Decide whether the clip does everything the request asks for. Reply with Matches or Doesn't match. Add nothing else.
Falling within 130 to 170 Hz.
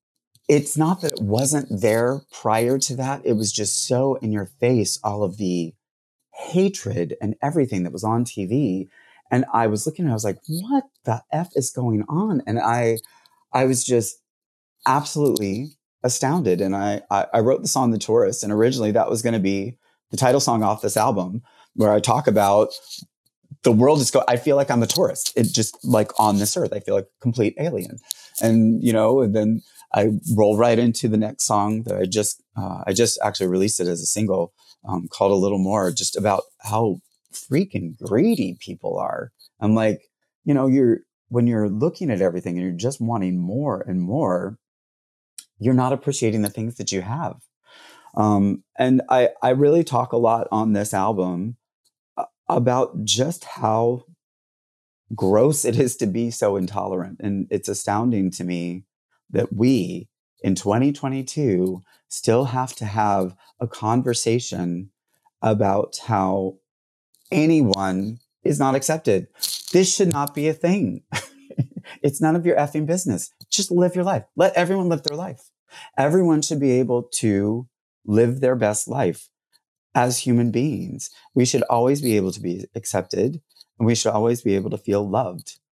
Doesn't match